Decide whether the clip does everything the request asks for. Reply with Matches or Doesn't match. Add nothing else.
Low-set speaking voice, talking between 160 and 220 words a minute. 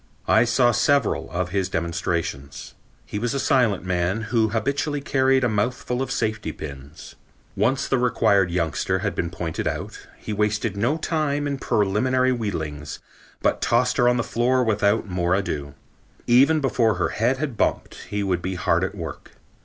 Matches